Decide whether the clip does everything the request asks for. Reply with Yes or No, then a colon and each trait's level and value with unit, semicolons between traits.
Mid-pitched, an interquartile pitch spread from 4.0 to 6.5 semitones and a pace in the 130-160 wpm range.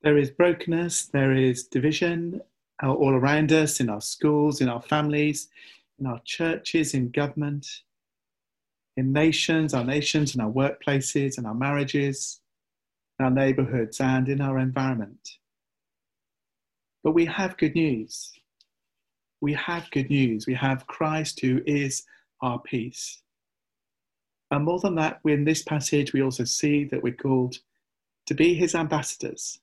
No: medium, 145 Hz; average, 2.9 semitones; average, 140 wpm